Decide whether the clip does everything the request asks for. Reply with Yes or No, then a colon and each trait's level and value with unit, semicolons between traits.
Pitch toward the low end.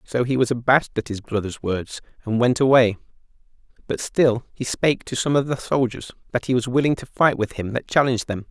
Yes: low, 125 Hz